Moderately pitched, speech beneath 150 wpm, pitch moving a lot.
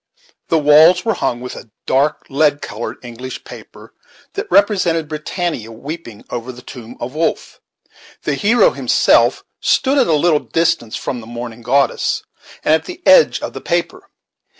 No: medium, 150 Hz; average, 160 wpm; wide, 5.7 semitones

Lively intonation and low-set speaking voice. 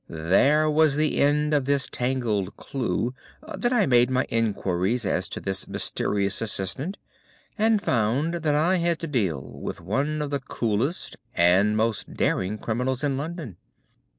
Yes: wide, 6.6 semitones; low, 130 Hz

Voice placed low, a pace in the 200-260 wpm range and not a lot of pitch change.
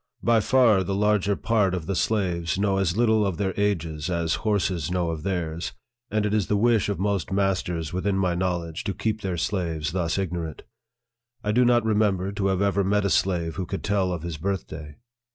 No: very low, 95 Hz; fast, 205 wpm; average, 3.1 semitones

